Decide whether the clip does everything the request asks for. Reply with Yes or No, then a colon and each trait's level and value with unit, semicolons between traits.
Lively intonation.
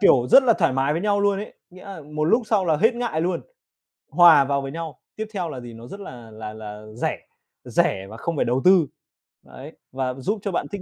Yes: wide, 7.5 semitones